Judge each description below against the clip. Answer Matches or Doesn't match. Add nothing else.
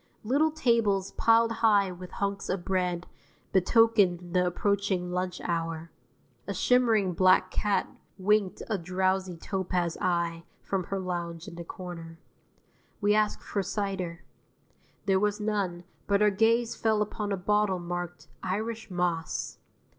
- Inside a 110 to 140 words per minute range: Matches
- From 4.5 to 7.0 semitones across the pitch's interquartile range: Doesn't match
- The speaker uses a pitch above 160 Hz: Matches